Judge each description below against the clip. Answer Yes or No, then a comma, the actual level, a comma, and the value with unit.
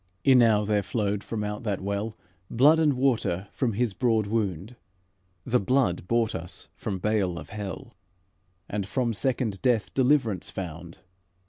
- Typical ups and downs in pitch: Yes, average, 3.8 semitones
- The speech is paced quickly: No, average, 145 wpm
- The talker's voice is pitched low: Yes, low, 105 Hz